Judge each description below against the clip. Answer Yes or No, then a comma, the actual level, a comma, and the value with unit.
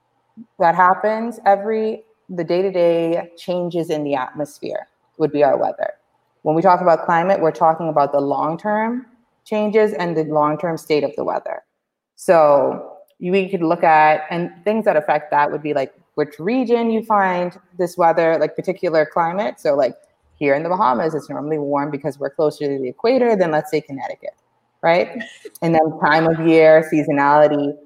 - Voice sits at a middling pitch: Yes, medium, 165 Hz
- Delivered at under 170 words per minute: No, average, 175 wpm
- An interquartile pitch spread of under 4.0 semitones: No, average, 4.4 semitones